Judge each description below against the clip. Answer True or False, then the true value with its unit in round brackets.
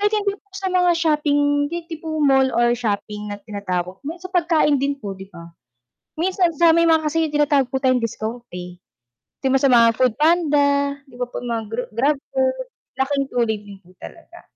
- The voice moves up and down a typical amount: False (6.3 semitones)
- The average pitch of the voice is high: True (280 Hz)